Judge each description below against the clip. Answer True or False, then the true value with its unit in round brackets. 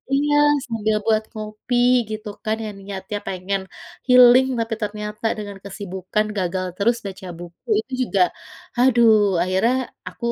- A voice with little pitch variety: False (3.2 semitones)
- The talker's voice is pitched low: False (215 Hz)